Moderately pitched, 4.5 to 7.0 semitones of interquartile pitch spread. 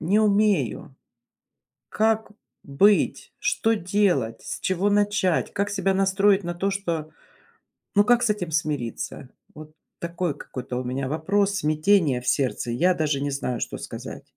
Yes: medium, 180 Hz; wide, 5.4 semitones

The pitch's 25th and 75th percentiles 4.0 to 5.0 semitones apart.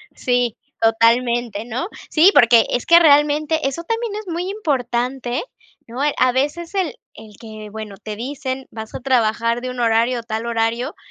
Yes: average, 4.4 semitones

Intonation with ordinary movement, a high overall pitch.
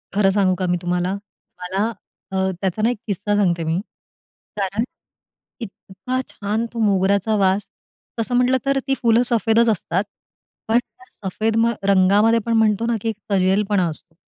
Yes: average, 3.3 semitones; high, 205 Hz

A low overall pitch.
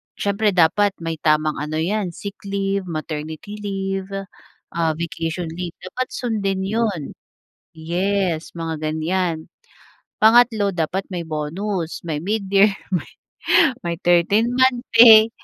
No: medium, 185 Hz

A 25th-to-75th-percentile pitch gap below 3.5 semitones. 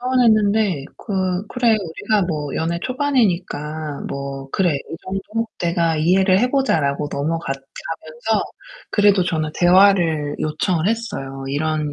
No: average, 5.2 semitones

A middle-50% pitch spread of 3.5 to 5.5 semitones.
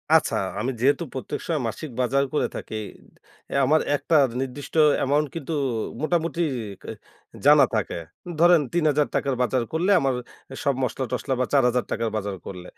Yes: average, 4.0 semitones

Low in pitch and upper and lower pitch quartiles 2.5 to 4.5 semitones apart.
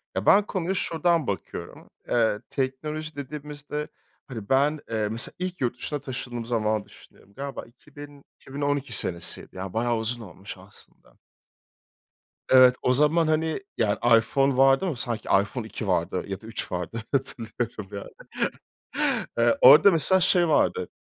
No: low, 130 Hz; average, 5.0 semitones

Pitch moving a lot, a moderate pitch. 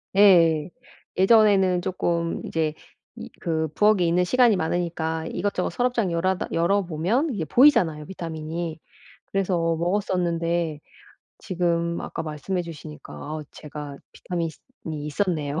No: average, 3.0 semitones; medium, 170 Hz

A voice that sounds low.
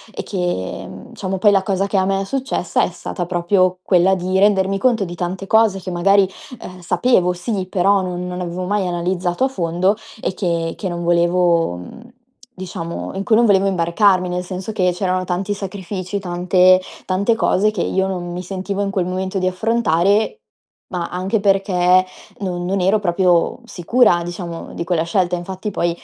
No: medium, 185 Hz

